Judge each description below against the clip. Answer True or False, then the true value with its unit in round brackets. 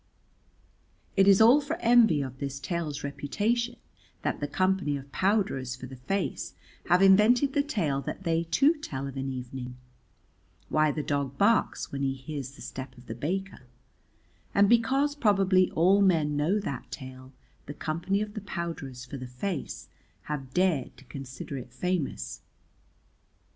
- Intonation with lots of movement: True (6.7 semitones)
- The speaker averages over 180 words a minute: False (160 wpm)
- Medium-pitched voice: True (155 Hz)